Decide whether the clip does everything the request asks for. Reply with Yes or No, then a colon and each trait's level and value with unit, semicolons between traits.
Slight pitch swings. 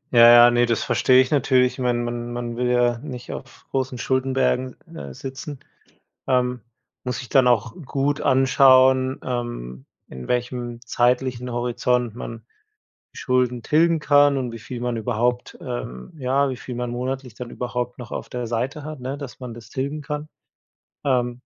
Yes: narrow, 1.7 semitones